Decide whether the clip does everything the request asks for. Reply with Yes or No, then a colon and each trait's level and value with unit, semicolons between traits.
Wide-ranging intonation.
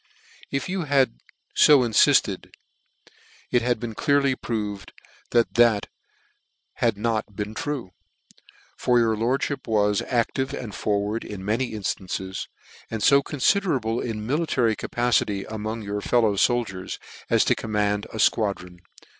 No: average, 3.4 semitones